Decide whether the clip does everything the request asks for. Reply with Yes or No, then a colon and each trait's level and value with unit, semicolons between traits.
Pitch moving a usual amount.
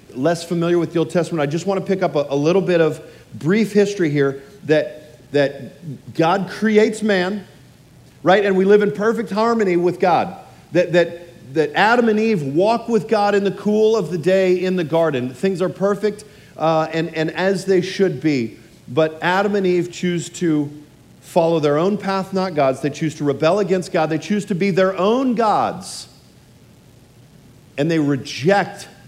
Yes: average, 4.2 semitones